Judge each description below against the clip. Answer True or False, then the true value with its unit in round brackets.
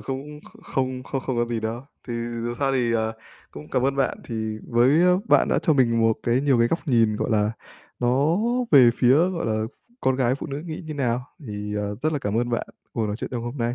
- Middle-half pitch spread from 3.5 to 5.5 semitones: False (3.0 semitones)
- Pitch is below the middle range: True (120 Hz)